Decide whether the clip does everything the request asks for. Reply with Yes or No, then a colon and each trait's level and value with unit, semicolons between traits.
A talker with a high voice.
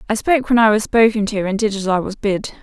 Yes: high, 210 Hz